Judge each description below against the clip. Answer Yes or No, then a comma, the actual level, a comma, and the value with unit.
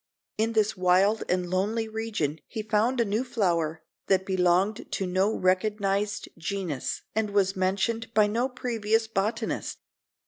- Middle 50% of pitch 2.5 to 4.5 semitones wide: Yes, average, 3.0 semitones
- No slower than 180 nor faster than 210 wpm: No, average, 140 wpm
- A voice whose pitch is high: Yes, high, 205 Hz